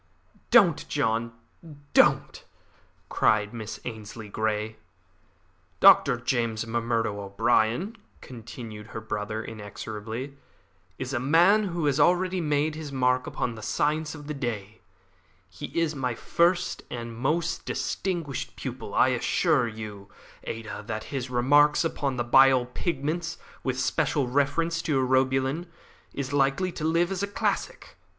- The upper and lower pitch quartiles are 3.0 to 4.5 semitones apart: No, average, 5.2 semitones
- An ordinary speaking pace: No, slow, 130 wpm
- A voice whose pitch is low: Yes, low, 130 Hz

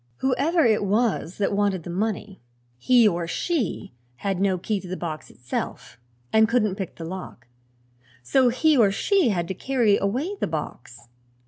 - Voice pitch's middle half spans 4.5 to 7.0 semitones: Yes, wide, 5.5 semitones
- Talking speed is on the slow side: No, average, 165 wpm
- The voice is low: No, high, 200 Hz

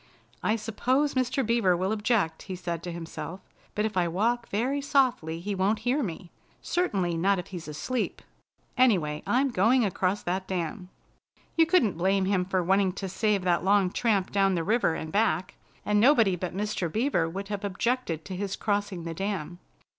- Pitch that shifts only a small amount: No, average, 4.0 semitones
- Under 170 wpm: No, average, 180 wpm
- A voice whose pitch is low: No, high, 195 Hz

